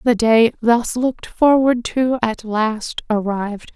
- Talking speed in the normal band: Yes, average, 145 wpm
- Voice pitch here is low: No, high, 230 Hz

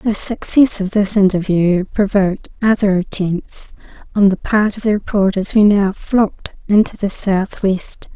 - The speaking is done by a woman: Yes, female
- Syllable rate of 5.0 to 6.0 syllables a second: No, 4.3 syllables/s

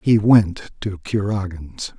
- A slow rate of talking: Yes, slow, 120 wpm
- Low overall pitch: Yes, low, 100 Hz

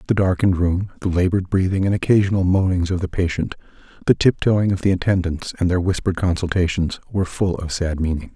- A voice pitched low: Yes, very low, 90 Hz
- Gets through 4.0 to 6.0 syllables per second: No, 6.3 syllables/s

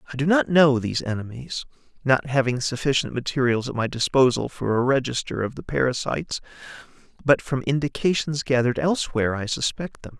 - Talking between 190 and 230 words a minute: No, average, 160 wpm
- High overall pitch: No, low, 130 Hz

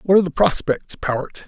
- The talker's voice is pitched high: No, medium, 165 Hz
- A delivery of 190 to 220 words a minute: Yes, fast, 205 wpm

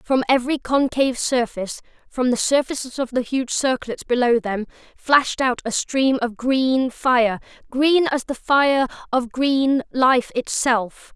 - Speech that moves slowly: No, average, 145 wpm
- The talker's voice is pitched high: Yes, very high, 255 Hz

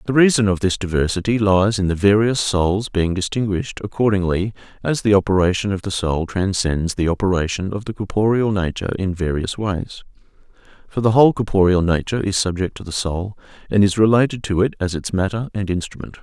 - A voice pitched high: No, low, 100 Hz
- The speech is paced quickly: No, average, 180 wpm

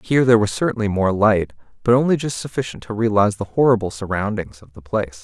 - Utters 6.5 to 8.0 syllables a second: Yes, 6.7 syllables/s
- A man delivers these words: Yes, male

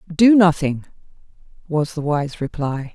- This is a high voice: No, medium, 160 Hz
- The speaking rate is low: Yes, slow, 120 wpm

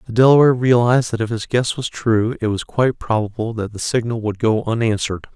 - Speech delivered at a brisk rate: Yes, fast, 215 wpm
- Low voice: Yes, low, 115 Hz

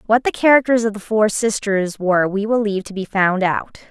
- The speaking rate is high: Yes, fast, 230 wpm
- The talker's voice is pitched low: No, high, 210 Hz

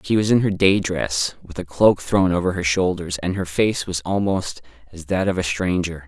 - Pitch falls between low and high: No, very low, 90 Hz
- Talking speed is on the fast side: Yes, fast, 225 wpm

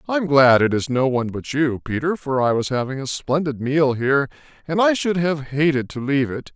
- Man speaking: Yes, male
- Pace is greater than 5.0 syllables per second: Yes, 5.5 syllables/s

